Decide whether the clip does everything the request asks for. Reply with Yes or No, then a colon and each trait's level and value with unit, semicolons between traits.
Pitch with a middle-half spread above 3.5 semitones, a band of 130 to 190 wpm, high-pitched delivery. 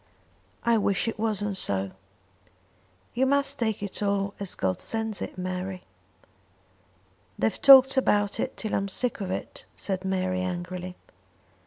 No: average, 3.2 semitones; average, 140 wpm; high, 200 Hz